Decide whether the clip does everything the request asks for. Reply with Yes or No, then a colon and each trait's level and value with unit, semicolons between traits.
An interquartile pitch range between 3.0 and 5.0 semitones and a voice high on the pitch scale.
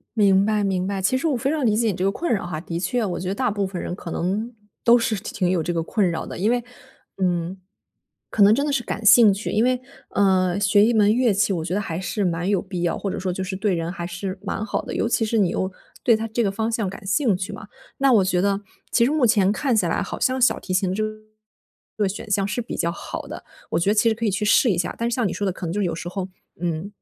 Yes: average, 3.4 semitones; high, 200 Hz